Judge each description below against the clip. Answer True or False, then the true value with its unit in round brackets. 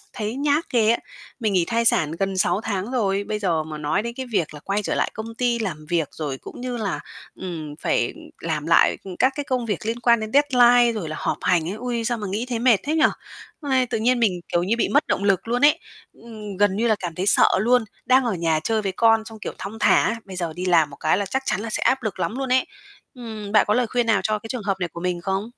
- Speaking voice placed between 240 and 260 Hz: False (215 Hz)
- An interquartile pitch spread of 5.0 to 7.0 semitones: False (4.6 semitones)